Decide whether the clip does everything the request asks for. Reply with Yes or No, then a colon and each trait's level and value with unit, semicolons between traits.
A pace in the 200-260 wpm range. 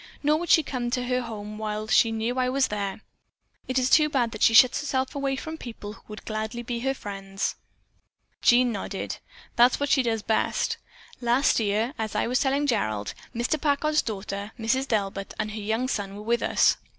Yes: fast, 205 wpm